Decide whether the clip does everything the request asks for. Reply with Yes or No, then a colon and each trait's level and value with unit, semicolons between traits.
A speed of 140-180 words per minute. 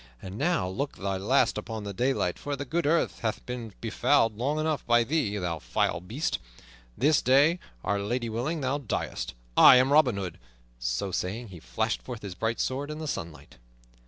No: average, 190 wpm